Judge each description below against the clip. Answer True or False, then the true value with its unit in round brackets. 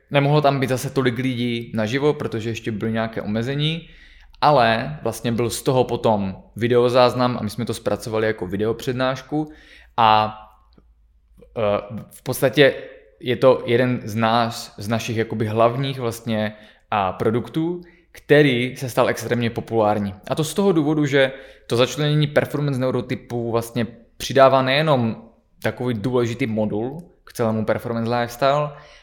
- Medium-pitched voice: False (120 Hz)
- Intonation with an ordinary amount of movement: True (3.5 semitones)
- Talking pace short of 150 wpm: True (135 wpm)